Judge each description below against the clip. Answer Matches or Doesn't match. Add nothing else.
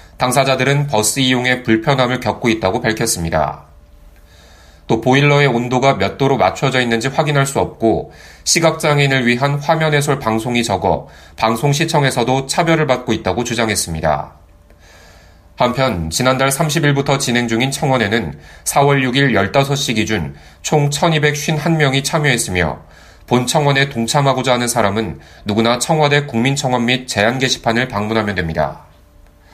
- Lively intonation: Matches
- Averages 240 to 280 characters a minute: Doesn't match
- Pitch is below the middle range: Matches